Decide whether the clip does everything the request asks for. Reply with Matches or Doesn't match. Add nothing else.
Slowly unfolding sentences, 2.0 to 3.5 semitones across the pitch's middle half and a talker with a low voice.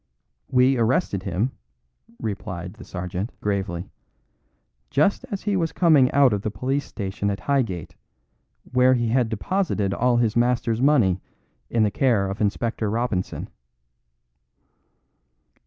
Doesn't match